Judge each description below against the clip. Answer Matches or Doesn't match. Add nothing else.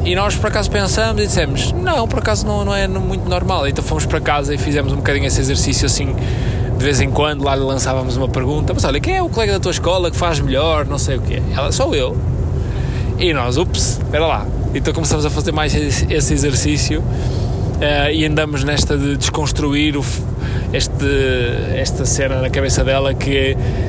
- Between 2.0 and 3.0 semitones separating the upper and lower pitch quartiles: Matches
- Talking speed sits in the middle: Doesn't match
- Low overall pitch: Matches